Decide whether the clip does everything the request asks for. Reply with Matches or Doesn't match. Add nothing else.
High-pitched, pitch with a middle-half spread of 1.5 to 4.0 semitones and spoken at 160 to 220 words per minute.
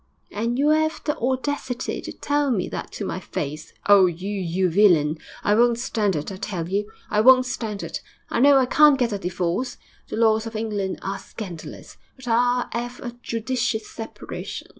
Doesn't match